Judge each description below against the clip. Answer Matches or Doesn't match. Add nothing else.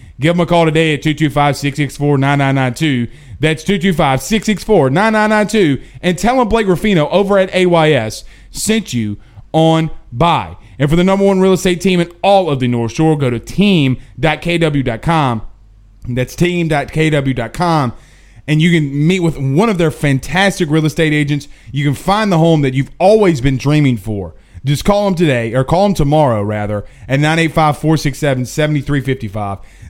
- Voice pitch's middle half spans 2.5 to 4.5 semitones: Doesn't match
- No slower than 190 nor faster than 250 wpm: Doesn't match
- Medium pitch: Matches